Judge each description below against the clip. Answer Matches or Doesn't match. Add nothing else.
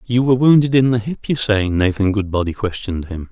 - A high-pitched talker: Doesn't match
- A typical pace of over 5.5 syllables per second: Matches